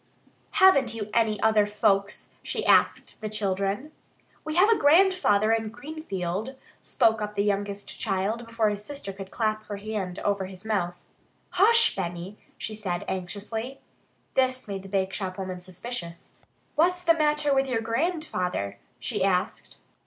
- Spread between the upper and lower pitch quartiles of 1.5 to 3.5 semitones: No, average, 5.1 semitones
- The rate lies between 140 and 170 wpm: Yes, average, 145 wpm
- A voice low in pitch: No, high, 210 Hz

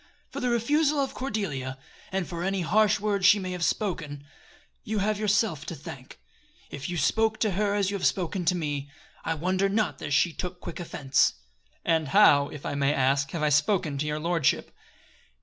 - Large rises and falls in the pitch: Yes, wide, 5.7 semitones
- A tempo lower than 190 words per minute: No, average, 195 wpm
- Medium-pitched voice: Yes, medium, 175 Hz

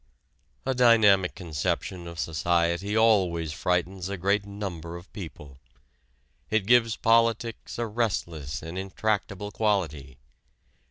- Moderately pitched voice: No, very low, 95 Hz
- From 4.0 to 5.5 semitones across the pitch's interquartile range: Yes, average, 4.4 semitones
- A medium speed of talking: No, slow, 110 wpm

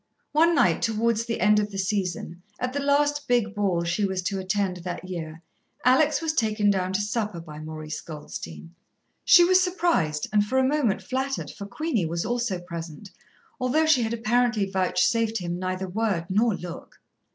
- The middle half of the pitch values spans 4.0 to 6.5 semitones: Yes, wide, 5.5 semitones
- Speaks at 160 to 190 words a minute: Yes, average, 175 wpm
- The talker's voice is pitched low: No, high, 205 Hz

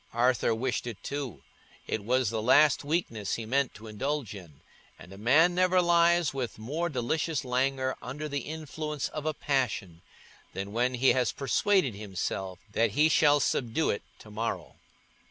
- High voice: No, low, 130 Hz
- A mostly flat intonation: No, average, 5.3 semitones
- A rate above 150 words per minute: Yes, average, 165 wpm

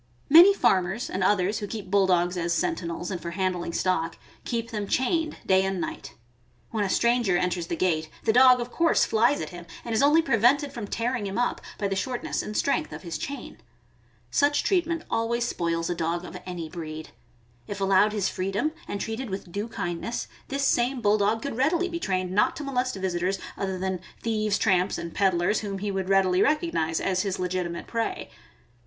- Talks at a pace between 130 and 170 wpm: No, average, 195 wpm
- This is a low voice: No, high, 200 Hz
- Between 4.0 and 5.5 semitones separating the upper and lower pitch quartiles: Yes, average, 4.9 semitones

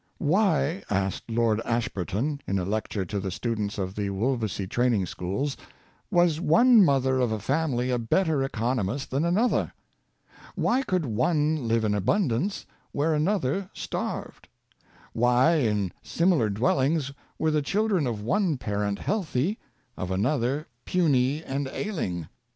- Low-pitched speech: Yes, low, 130 Hz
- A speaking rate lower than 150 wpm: Yes, average, 140 wpm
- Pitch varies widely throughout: Yes, wide, 6.9 semitones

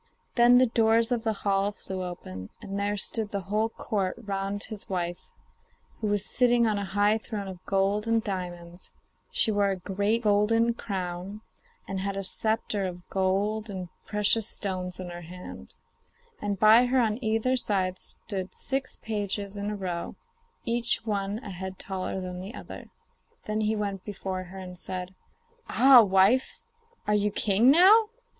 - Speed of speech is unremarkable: Yes, average, 165 wpm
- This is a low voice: No, high, 205 Hz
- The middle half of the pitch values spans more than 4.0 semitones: No, average, 2.7 semitones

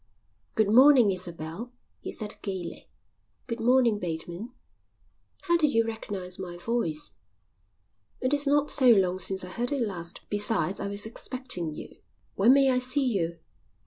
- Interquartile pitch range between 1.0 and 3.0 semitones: No, wide, 5.6 semitones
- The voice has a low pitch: No, high, 215 Hz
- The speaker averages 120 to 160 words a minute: Yes, average, 150 wpm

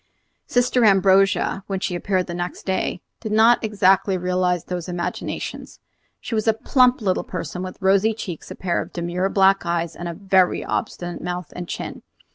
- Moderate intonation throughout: No, narrow, 2.1 semitones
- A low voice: No, medium, 185 Hz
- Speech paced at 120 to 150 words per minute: No, average, 170 wpm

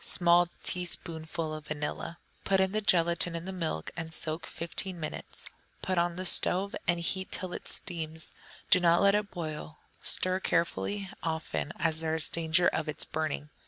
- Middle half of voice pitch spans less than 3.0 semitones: Yes, narrow, 2.5 semitones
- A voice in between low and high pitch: Yes, medium, 170 Hz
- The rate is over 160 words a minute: Yes, average, 170 wpm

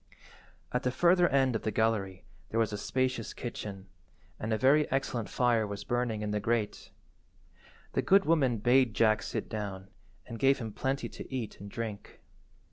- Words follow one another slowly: No, average, 175 wpm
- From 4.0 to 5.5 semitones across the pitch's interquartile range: No, average, 3.6 semitones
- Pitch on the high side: No, low, 115 Hz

